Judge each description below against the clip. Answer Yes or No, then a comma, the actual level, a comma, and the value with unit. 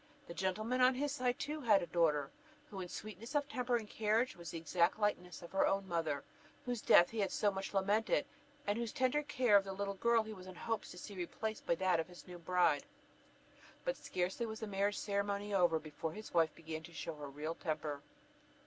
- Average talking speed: No, fast, 220 wpm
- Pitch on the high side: Yes, high, 195 Hz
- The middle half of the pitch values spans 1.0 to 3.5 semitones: No, average, 4.5 semitones